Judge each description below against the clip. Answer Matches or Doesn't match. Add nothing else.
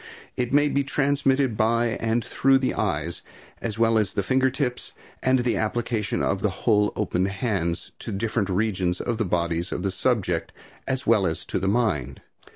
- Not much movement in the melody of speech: Doesn't match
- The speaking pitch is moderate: Doesn't match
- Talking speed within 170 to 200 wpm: Matches